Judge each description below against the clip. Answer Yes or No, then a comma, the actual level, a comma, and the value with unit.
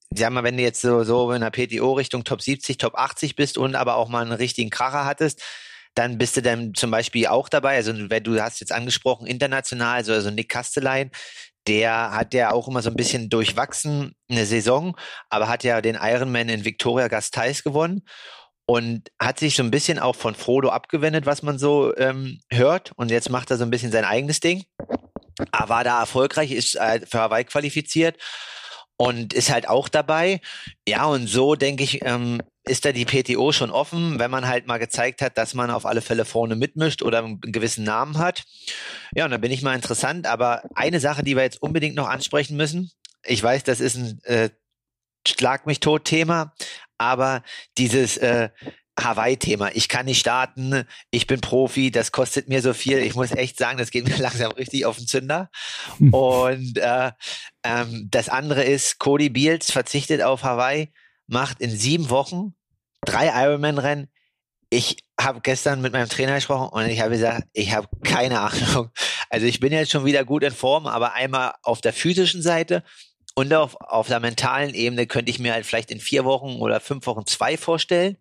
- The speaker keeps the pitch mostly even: No, average, 3.3 semitones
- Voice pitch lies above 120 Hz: Yes, low, 130 Hz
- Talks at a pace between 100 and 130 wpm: No, fast, 190 wpm